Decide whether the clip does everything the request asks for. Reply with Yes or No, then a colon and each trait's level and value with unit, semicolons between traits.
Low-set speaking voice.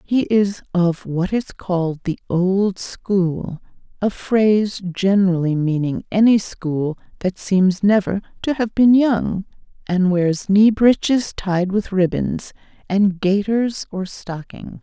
No: high, 195 Hz